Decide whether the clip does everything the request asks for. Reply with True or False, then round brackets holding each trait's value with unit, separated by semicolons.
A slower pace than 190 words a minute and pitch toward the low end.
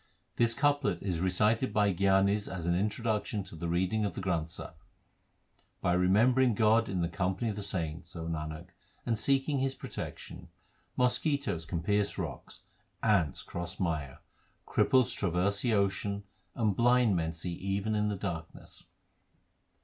True (150 wpm; 100 Hz)